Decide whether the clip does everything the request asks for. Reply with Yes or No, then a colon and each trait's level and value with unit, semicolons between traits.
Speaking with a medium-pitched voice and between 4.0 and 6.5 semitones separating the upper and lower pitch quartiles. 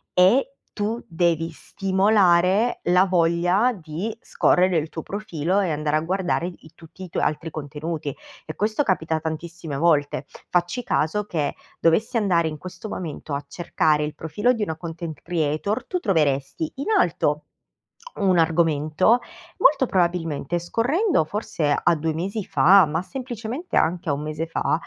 Yes: medium, 170 Hz; average, 4.4 semitones